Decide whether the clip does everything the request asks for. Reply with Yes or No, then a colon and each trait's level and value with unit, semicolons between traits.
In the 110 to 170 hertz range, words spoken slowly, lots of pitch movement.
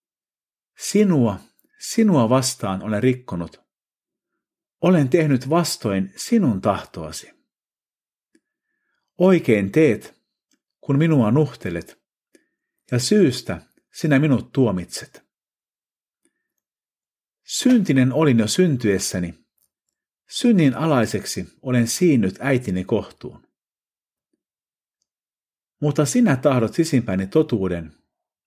Yes: low, 130 Hz; slow, 75 wpm; wide, 7.8 semitones